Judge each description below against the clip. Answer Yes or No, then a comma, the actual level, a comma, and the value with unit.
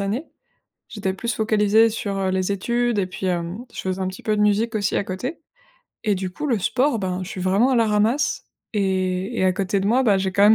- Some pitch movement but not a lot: Yes, average, 3.1 semitones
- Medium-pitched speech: No, high, 200 Hz